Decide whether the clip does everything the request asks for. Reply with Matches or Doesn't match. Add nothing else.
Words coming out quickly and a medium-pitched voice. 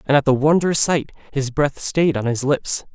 Matches